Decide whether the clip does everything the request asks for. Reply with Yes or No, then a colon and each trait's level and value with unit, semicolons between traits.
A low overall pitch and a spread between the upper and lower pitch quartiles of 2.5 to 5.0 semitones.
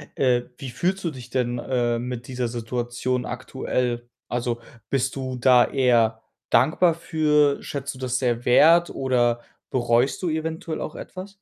Yes: low, 125 Hz; average, 2.8 semitones